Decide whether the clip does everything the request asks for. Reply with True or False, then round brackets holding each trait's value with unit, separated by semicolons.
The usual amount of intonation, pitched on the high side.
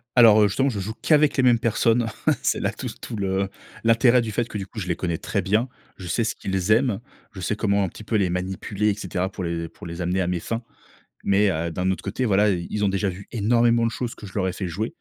False (3.6 semitones; 100 Hz)